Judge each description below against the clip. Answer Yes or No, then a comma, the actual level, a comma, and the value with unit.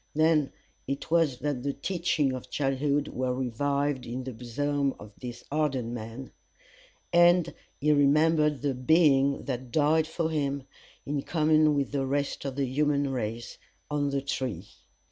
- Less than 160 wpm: Yes, average, 150 wpm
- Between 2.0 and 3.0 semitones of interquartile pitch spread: Yes, narrow, 2.6 semitones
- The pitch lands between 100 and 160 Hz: Yes, medium, 140 Hz